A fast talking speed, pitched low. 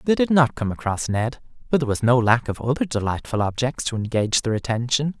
Yes: fast, 220 wpm; low, 125 Hz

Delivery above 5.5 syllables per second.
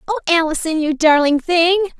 No: 5.2 syllables/s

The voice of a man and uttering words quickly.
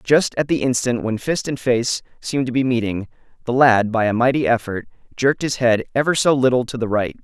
Yes: male; fast, 225 wpm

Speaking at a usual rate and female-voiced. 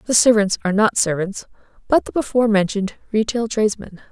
Yes: average, 160 wpm; female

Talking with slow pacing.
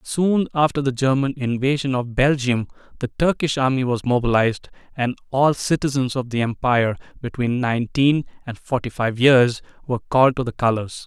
No: average, 155 wpm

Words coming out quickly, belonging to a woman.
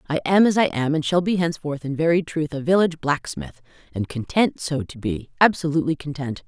No: average, 185 wpm; female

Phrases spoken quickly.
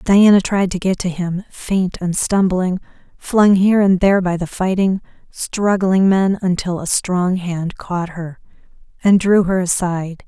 No: average, 165 wpm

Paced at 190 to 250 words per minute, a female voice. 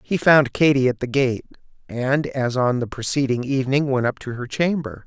No: average, 200 wpm; male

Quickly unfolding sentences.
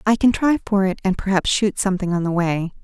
Yes: fast, 255 wpm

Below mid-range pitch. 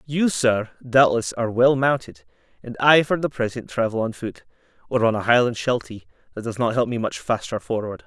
Yes: low, 120 Hz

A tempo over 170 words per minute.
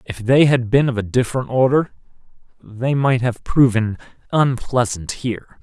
No: average, 150 wpm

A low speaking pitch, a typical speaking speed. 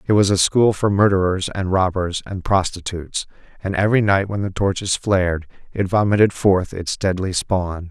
Yes: very low, 95 Hz; average, 175 wpm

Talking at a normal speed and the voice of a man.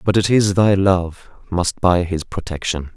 Yes: average, 180 wpm; male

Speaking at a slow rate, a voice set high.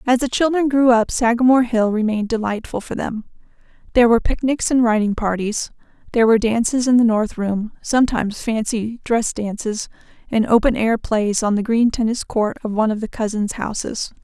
No: average, 175 wpm; high, 230 Hz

